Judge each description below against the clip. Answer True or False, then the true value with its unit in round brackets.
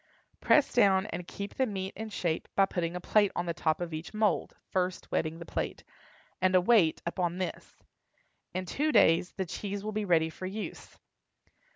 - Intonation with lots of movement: False (3.0 semitones)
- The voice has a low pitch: False (185 Hz)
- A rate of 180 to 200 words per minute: True (190 wpm)